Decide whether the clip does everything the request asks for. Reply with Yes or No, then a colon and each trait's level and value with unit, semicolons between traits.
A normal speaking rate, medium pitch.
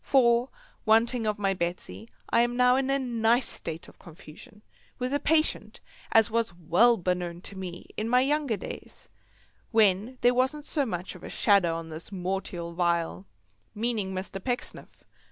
No: average, 160 wpm; high, 215 Hz